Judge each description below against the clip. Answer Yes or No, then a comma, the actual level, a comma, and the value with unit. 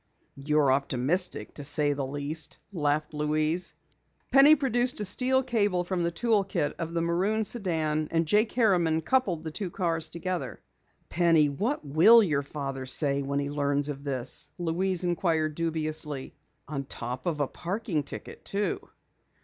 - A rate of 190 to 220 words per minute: No, average, 155 wpm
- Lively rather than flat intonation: No, average, 4.4 semitones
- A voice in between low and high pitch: Yes, medium, 160 Hz